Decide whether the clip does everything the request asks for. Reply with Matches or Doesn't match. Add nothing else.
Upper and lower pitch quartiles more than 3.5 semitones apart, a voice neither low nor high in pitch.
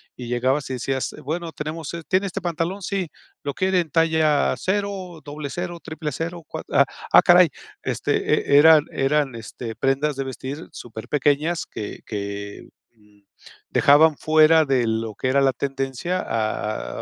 Matches